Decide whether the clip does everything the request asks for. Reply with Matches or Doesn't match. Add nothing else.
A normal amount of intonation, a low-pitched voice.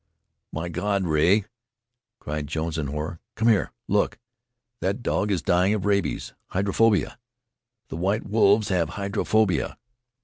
Matches